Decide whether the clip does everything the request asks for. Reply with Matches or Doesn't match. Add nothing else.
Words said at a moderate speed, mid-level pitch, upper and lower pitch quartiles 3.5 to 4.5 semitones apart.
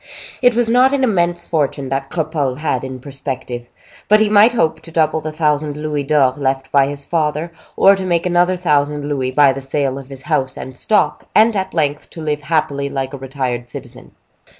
Matches